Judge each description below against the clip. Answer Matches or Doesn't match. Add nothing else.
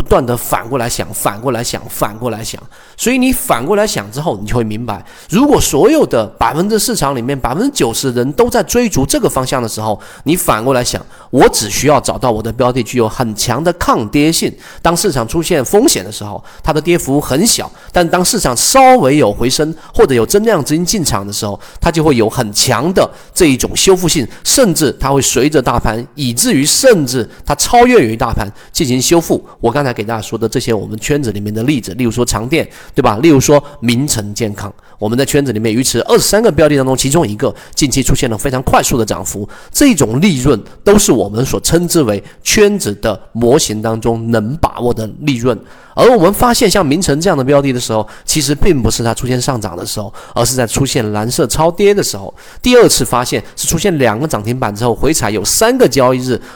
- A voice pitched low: Matches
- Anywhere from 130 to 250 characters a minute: Doesn't match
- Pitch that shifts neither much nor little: Doesn't match